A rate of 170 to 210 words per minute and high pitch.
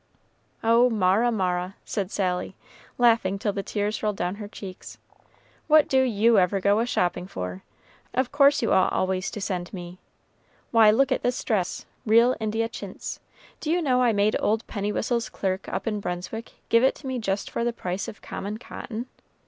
Yes: average, 180 wpm; high, 210 Hz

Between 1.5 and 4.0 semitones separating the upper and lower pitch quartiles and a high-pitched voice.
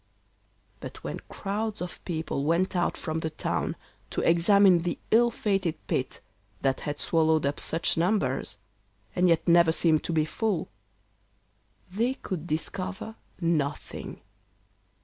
No: average, 3.5 semitones; medium, 170 Hz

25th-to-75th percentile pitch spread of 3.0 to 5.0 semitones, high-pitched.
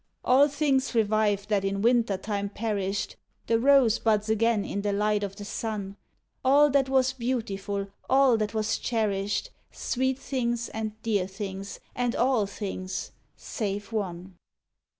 Yes: average, 3.5 semitones; high, 215 Hz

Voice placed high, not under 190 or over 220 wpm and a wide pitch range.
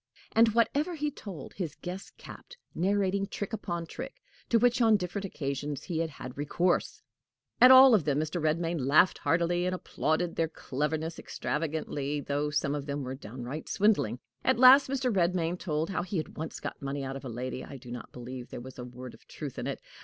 No: medium, 165 Hz; average, 200 wpm; wide, 6.0 semitones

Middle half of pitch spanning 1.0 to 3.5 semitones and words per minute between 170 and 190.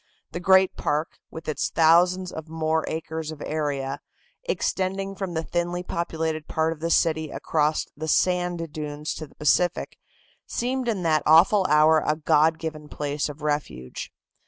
No: narrow, 2.5 semitones; average, 155 wpm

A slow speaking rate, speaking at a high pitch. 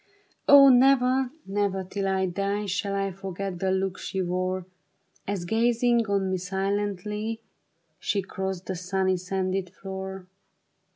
Yes: slow, 130 wpm; high, 195 Hz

